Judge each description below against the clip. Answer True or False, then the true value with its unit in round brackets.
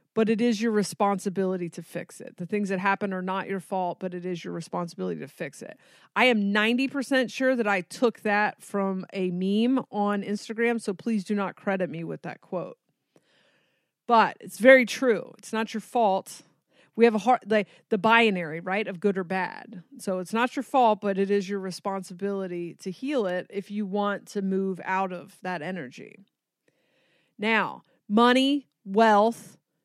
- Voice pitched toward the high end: True (205 Hz)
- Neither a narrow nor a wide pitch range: True (3.3 semitones)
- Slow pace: False (185 wpm)